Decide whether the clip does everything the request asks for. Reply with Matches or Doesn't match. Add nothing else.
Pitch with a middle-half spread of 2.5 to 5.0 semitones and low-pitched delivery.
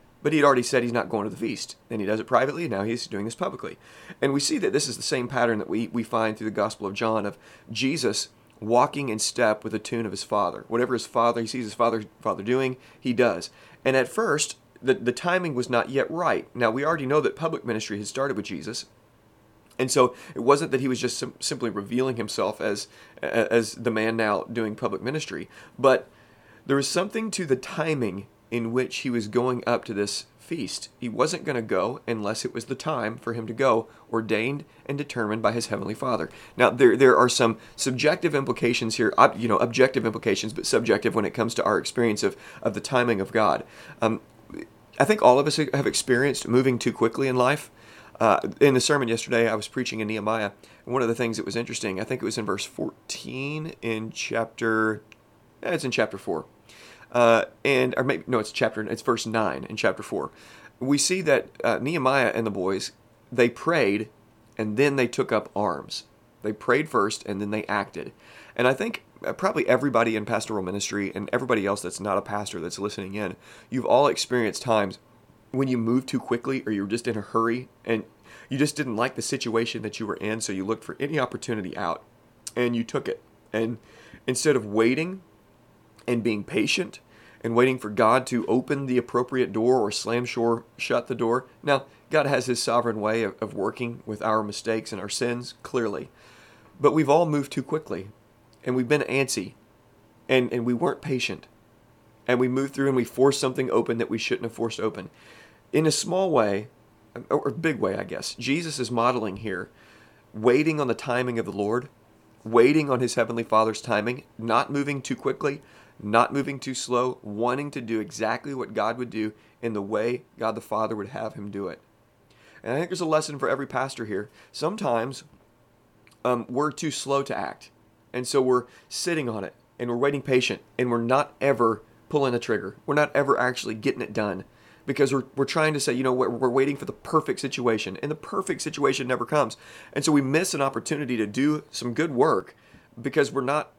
Matches